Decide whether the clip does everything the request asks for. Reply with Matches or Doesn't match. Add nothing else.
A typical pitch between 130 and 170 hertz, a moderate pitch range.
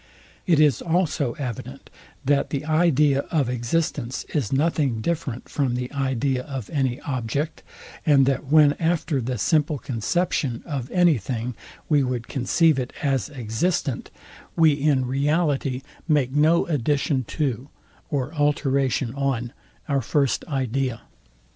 Matches